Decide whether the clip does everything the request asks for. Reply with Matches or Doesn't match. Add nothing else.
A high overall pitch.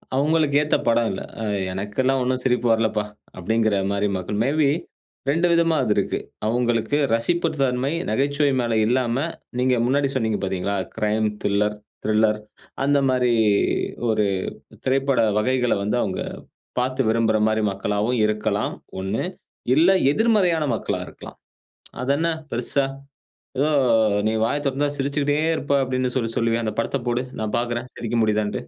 Doesn't match